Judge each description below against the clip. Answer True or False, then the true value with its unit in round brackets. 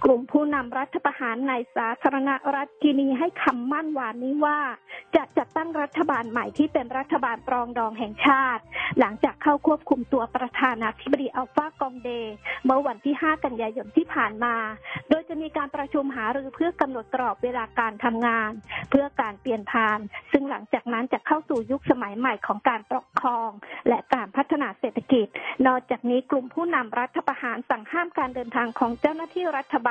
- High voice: True (265 Hz)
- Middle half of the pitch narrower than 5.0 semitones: True (3.6 semitones)